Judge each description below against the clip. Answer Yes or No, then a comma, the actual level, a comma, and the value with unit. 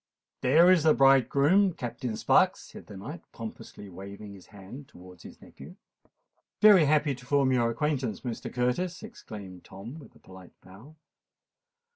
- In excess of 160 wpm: No, average, 150 wpm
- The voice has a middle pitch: No, low, 125 Hz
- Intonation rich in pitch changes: Yes, wide, 6.8 semitones